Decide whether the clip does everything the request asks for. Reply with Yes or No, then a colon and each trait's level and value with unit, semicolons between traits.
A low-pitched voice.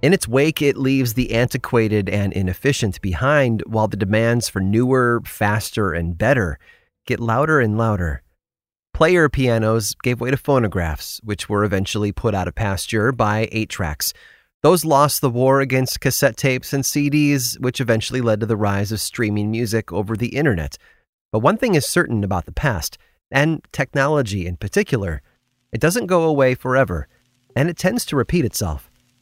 Yes: low, 120 Hz